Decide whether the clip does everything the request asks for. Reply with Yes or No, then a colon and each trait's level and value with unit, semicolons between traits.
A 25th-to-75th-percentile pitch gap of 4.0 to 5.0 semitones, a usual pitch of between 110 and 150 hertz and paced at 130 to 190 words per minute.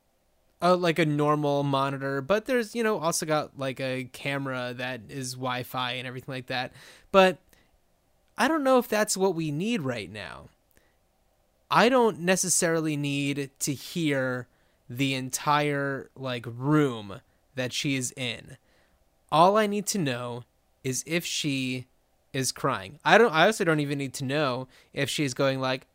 Yes: average, 4.3 semitones; medium, 140 Hz; average, 160 wpm